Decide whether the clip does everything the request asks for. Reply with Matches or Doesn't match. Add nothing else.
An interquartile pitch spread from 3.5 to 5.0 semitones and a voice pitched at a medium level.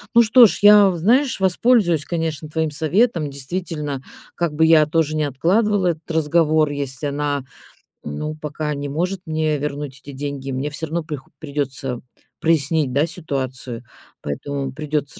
Doesn't match